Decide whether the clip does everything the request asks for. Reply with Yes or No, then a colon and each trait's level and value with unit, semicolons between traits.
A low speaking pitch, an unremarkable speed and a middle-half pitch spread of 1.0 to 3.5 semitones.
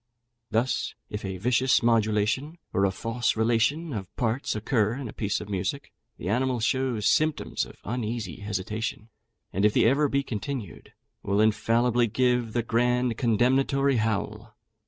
Yes: low, 115 Hz; average, 150 wpm; average, 3.2 semitones